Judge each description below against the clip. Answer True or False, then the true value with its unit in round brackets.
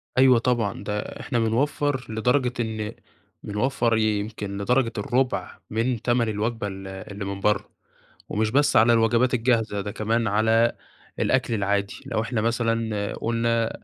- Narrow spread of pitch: True (2.3 semitones)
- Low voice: True (115 Hz)